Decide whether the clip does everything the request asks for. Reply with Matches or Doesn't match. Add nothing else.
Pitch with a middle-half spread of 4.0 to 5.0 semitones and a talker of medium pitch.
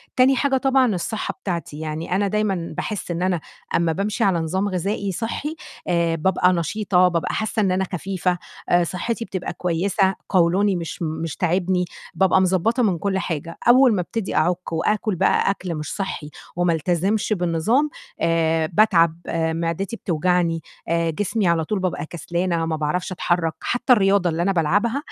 Doesn't match